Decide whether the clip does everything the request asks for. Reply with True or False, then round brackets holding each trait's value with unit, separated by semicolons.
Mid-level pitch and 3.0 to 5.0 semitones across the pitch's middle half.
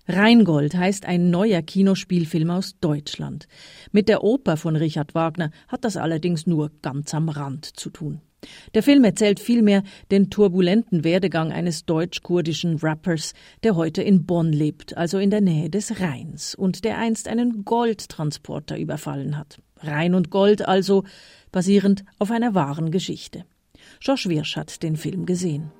True (180 Hz; 3.9 semitones)